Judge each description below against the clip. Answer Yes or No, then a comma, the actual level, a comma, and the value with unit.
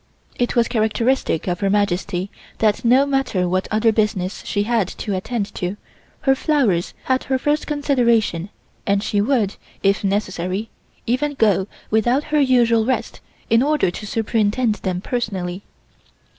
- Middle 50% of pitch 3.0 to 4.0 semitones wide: No, average, 4.4 semitones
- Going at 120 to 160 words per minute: Yes, average, 145 wpm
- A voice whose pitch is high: Yes, high, 220 Hz